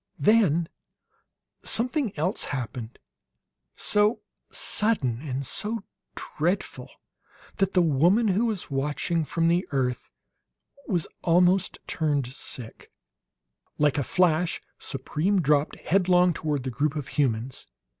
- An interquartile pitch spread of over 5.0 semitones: Yes, wide, 5.4 semitones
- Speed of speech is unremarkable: No, slow, 110 wpm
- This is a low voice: No, medium, 165 Hz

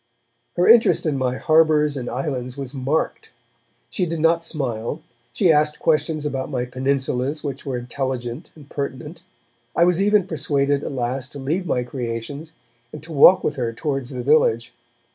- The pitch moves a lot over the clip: No, average, 3.7 semitones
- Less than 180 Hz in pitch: Yes, medium, 140 Hz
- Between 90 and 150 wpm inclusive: No, average, 165 wpm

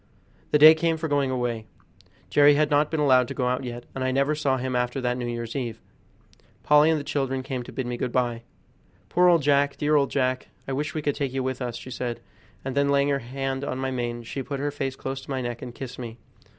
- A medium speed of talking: No, fast, 255 wpm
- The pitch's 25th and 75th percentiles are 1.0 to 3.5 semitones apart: Yes, narrow, 2.5 semitones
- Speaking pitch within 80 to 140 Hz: Yes, low, 135 Hz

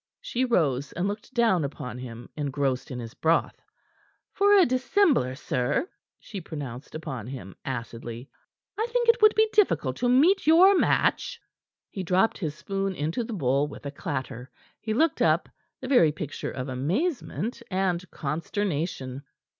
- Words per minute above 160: No, average, 155 wpm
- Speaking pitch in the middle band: Yes, medium, 165 Hz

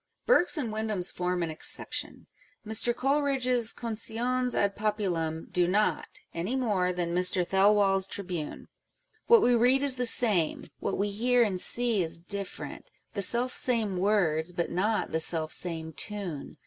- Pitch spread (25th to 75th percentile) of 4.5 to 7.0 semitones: Yes, average, 5.1 semitones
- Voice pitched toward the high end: Yes, high, 200 Hz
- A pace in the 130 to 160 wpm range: Yes, average, 155 wpm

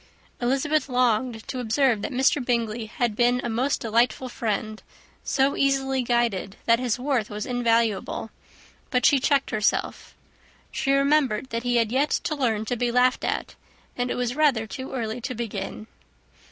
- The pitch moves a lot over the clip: No, average, 2.9 semitones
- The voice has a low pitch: No, high, 245 Hz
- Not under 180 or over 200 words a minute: No, average, 165 wpm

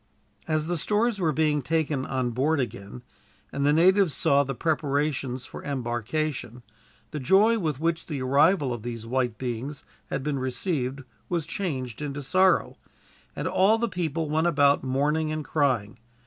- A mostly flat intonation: No, average, 4.0 semitones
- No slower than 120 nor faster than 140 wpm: No, average, 160 wpm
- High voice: No, medium, 145 Hz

